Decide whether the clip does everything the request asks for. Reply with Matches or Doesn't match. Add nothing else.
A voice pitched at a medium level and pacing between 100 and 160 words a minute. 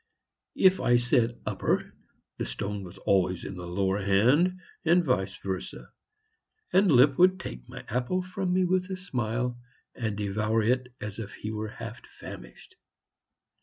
Doesn't match